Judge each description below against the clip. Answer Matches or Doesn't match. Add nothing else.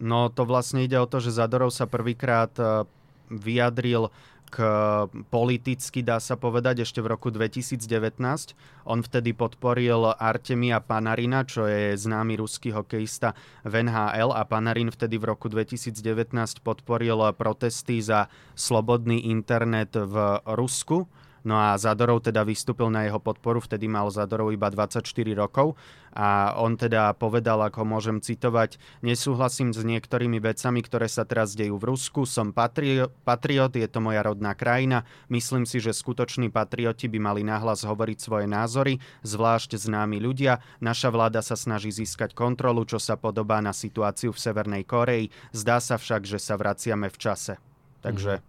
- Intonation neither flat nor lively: Doesn't match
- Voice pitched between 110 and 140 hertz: Matches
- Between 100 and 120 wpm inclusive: Doesn't match